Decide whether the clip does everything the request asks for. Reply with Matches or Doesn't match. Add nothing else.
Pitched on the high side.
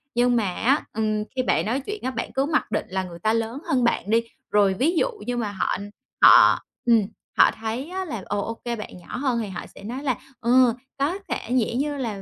Matches